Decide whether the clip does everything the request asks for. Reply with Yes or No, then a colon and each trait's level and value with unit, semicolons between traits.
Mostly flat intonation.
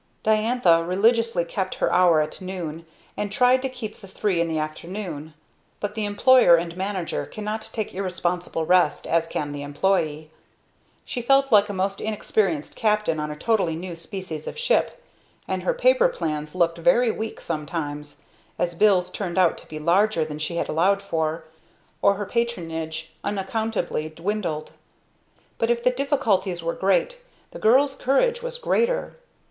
No: average, 5.1 semitones